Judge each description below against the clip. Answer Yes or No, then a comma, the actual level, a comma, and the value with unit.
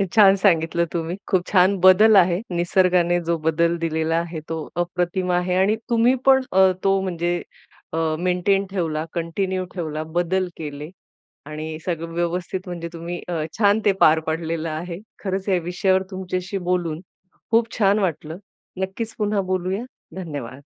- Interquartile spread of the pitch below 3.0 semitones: Yes, narrow, 2.4 semitones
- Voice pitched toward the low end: No, medium, 180 Hz